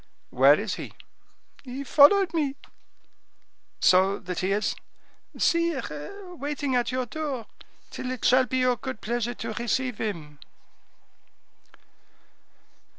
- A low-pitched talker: No, very high, 255 Hz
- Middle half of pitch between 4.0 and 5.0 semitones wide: Yes, average, 4.7 semitones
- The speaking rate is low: Yes, slow, 115 wpm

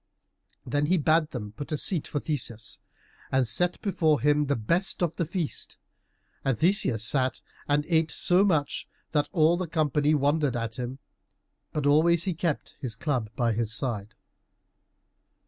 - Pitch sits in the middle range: Yes, medium, 150 Hz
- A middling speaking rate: Yes, average, 160 wpm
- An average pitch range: Yes, average, 4.5 semitones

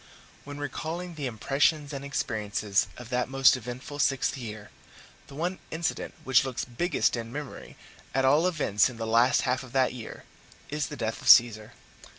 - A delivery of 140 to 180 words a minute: Yes, average, 170 wpm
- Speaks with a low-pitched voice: Yes, low, 130 Hz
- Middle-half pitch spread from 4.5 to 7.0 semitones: No, average, 3.7 semitones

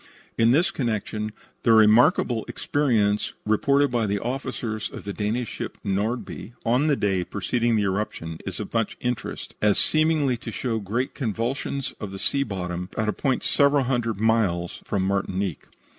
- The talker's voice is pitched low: Yes, low, 110 Hz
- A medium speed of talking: Yes, average, 160 wpm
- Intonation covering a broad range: No, average, 3.5 semitones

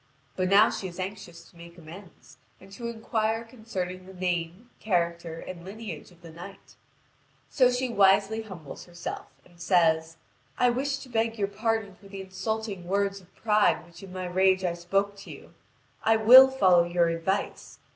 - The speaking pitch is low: No, high, 190 Hz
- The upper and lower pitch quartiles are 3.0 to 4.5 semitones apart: Yes, average, 4.0 semitones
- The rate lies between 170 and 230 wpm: Yes, average, 175 wpm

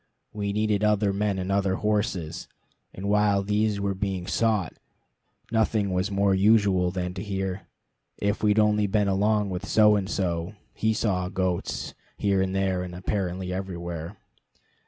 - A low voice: Yes, low, 100 Hz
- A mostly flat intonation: Yes, narrow, 2.0 semitones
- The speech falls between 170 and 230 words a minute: No, average, 155 wpm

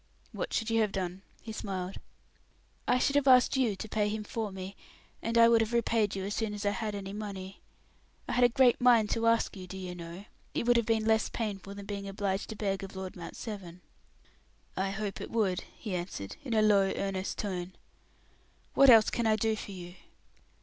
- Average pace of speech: No, fast, 215 wpm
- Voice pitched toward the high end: Yes, high, 205 Hz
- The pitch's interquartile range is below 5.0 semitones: Yes, average, 2.9 semitones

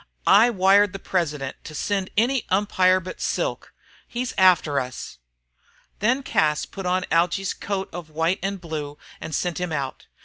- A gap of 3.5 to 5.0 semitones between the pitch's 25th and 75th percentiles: Yes, average, 3.9 semitones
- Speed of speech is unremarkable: Yes, average, 160 wpm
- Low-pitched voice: No, medium, 185 Hz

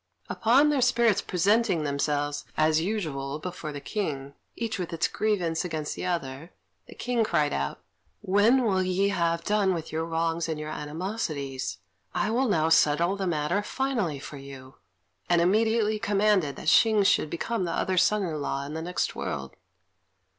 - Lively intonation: Yes, wide, 5.7 semitones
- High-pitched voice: No, medium, 170 Hz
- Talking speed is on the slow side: No, average, 170 wpm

